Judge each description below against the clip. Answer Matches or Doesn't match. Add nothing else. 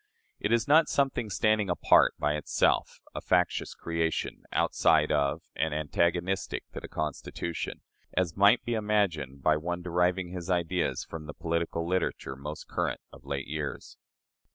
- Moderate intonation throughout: Matches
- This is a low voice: Matches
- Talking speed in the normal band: Matches